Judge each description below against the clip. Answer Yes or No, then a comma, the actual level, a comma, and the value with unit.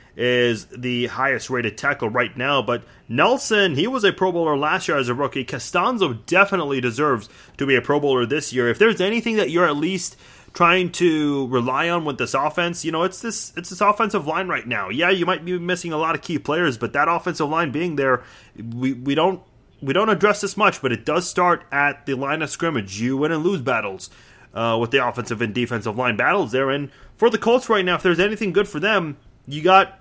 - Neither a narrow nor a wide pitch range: No, wide, 6.1 semitones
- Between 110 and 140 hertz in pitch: No, medium, 150 Hz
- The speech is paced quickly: Yes, fast, 220 wpm